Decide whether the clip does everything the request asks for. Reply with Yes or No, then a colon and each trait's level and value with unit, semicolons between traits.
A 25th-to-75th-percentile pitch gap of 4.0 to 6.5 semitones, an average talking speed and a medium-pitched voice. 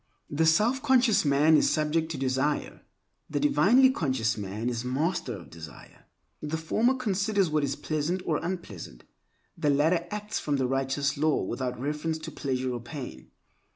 Yes: average, 5.2 semitones; average, 160 wpm; medium, 150 Hz